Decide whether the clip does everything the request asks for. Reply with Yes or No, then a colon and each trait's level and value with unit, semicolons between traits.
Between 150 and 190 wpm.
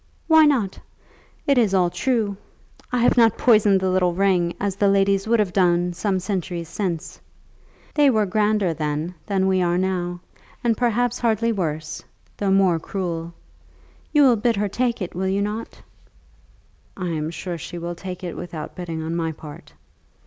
Yes: average, 170 wpm